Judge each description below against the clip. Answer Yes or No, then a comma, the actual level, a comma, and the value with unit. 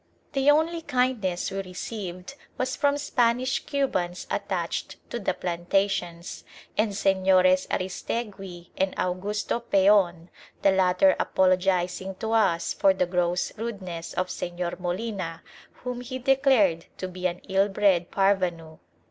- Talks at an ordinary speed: No, slow, 125 wpm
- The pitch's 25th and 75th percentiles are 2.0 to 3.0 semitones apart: No, average, 4.2 semitones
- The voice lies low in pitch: No, high, 190 Hz